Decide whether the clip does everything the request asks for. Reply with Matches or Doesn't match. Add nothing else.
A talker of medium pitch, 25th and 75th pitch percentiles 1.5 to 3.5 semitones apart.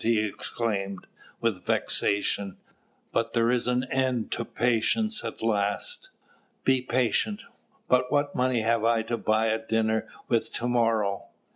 Doesn't match